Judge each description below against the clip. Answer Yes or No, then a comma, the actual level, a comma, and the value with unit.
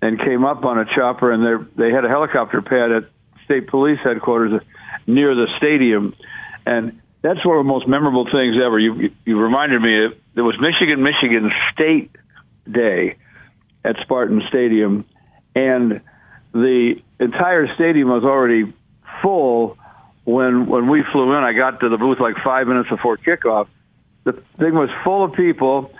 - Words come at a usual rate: Yes, average, 165 wpm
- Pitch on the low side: Yes, low, 125 Hz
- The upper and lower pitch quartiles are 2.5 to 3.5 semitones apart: Yes, average, 3.0 semitones